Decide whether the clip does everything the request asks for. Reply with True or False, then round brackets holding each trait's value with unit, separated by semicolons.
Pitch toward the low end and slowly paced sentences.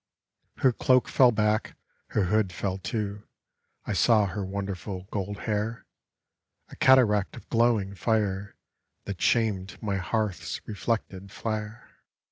True (105 Hz; 120 wpm)